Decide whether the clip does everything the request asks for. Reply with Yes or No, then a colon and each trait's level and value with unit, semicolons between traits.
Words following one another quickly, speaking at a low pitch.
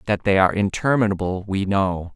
No: average, 165 wpm; low, 100 Hz